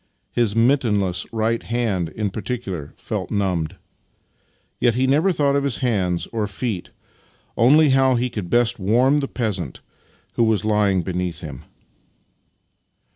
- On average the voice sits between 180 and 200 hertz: No, low, 110 Hz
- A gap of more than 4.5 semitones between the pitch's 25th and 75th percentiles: Yes, average, 4.9 semitones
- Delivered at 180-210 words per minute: No, average, 145 wpm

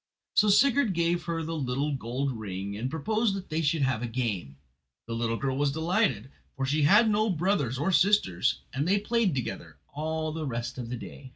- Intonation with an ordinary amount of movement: No, wide, 6.6 semitones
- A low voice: No, medium, 145 Hz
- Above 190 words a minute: Yes, average, 200 wpm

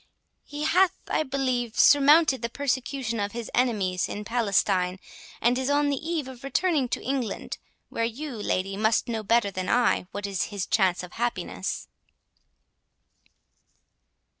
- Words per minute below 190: Yes, average, 145 wpm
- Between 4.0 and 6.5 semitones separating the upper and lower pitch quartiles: Yes, average, 5.1 semitones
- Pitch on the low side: No, high, 240 Hz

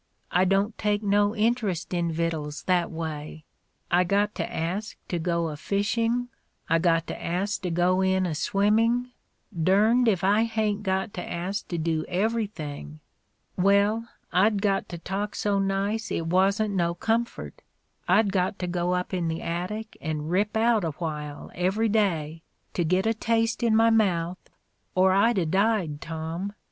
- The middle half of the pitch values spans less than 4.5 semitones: Yes, average, 3.9 semitones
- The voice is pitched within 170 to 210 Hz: Yes, high, 190 Hz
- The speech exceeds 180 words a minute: No, average, 170 wpm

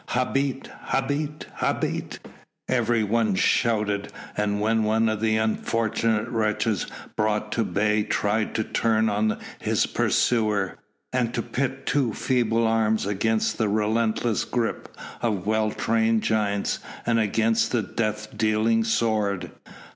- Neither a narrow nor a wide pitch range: No, narrow, 1.4 semitones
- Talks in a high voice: No, low, 110 Hz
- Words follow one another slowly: Yes, slow, 120 wpm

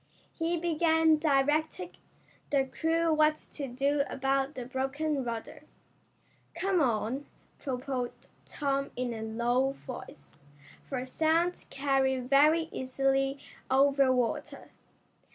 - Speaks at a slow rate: Yes, slow, 105 wpm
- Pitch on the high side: Yes, very high, 275 Hz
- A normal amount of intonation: Yes, average, 3.1 semitones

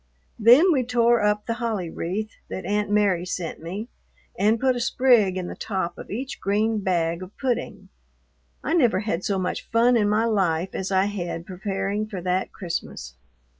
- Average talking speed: Yes, average, 180 wpm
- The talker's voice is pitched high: Yes, high, 205 Hz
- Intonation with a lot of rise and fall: No, average, 3.8 semitones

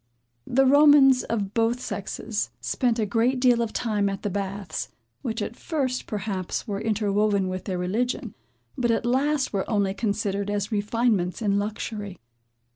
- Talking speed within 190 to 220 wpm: No, average, 155 wpm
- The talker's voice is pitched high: Yes, high, 215 Hz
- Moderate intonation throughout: Yes, average, 3.3 semitones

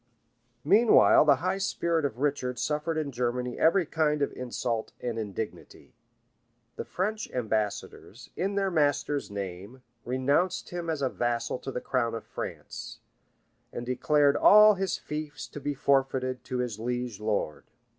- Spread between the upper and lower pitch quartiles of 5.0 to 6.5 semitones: No, average, 4.5 semitones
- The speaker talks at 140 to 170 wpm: Yes, average, 150 wpm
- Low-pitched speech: Yes, low, 130 Hz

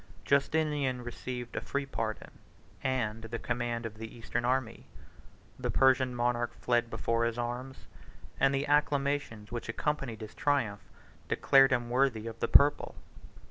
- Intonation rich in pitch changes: No, average, 2.8 semitones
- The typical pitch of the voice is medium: No, low, 120 Hz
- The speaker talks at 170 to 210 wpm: No, average, 140 wpm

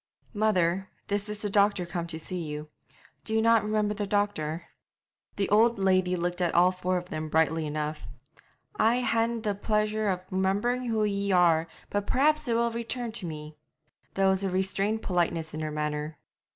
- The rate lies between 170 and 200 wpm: Yes, average, 180 wpm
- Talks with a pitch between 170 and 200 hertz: Yes, high, 190 Hz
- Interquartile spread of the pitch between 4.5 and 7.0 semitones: No, average, 4.1 semitones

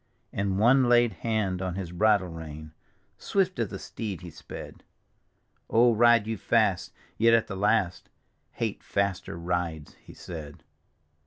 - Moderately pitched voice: No, low, 100 Hz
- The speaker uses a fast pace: No, average, 160 wpm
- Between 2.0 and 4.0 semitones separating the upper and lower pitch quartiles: No, average, 4.4 semitones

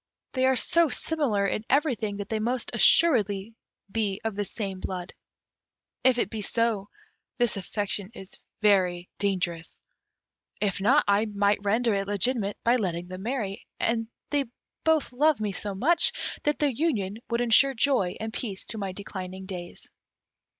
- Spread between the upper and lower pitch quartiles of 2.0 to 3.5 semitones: No, average, 4.1 semitones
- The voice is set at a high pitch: Yes, high, 210 Hz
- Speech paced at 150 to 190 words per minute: Yes, average, 155 wpm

